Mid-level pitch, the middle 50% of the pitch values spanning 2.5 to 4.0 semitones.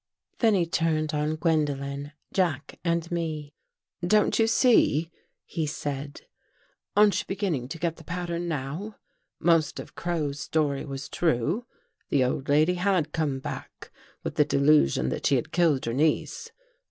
Yes: medium, 155 Hz; average, 3.3 semitones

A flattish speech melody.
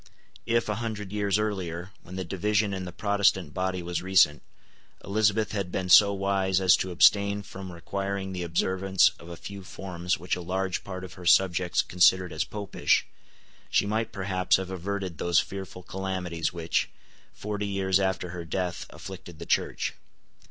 Yes: narrow, 1.8 semitones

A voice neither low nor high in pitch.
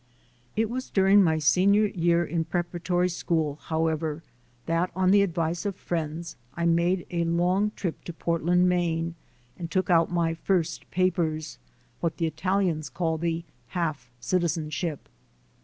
Yes: medium, 170 Hz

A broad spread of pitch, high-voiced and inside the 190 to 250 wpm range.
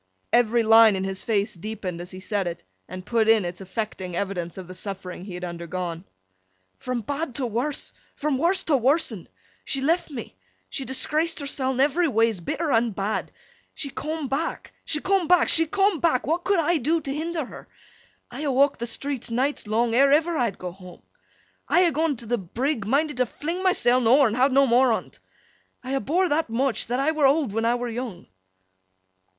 Yes: wide, 5.9 semitones; very high, 250 Hz; average, 200 wpm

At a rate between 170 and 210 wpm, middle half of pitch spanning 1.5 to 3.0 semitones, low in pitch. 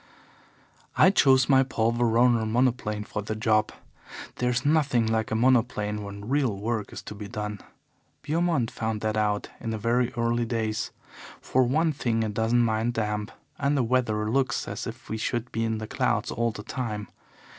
Yes: average, 175 wpm; narrow, 2.6 semitones; low, 115 Hz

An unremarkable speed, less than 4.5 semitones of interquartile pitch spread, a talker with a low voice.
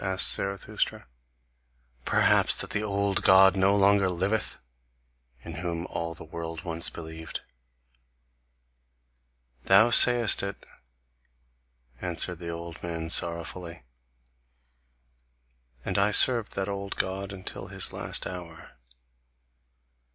No: slow, 105 wpm; average, 2.9 semitones; very low, 95 Hz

